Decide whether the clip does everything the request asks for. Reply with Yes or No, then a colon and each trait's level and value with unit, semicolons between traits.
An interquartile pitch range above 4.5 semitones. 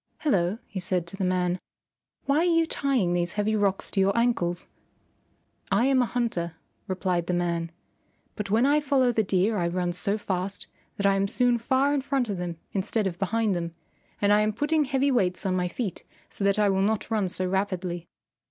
Yes: average, 4.9 semitones